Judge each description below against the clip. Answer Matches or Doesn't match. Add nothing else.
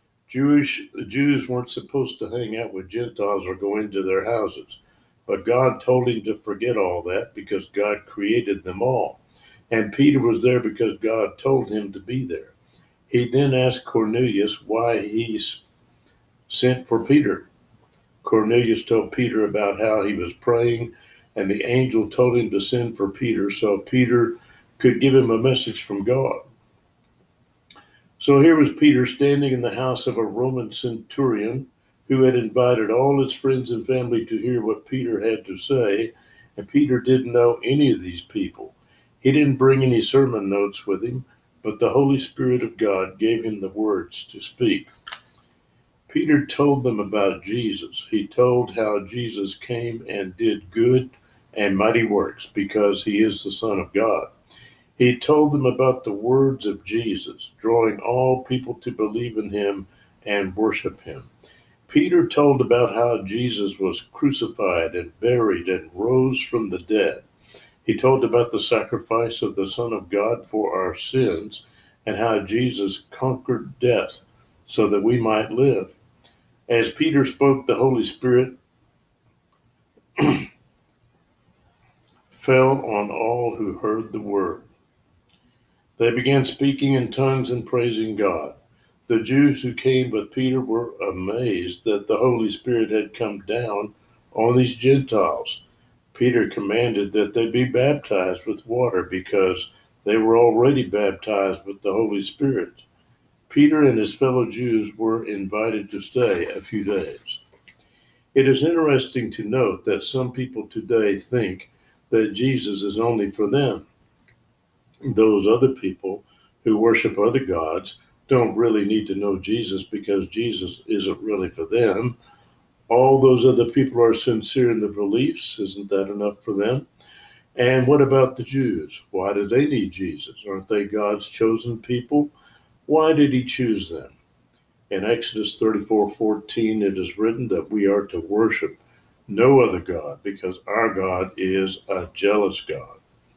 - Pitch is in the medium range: Doesn't match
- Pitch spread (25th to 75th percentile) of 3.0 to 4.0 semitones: Matches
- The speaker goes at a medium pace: Matches